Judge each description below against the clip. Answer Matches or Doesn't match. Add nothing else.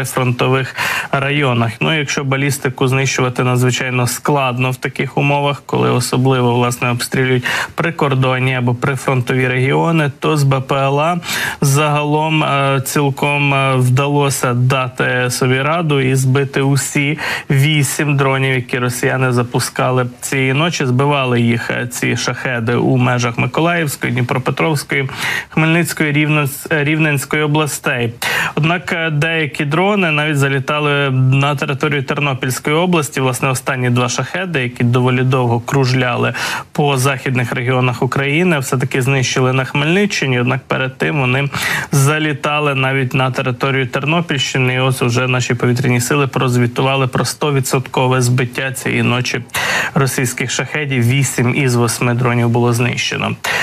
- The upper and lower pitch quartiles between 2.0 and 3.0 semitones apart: Matches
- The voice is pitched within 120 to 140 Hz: Matches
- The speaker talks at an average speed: Matches